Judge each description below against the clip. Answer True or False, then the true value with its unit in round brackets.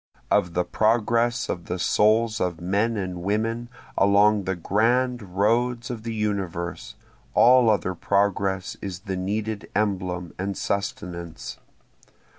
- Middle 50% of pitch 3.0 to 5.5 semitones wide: True (3.6 semitones)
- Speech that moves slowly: True (125 wpm)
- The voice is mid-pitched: False (100 Hz)